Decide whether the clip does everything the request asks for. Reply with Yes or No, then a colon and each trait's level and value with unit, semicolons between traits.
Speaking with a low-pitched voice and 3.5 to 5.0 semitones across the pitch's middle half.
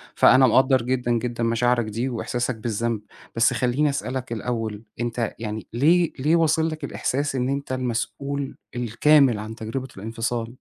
No: low, 125 Hz; average, 2.8 semitones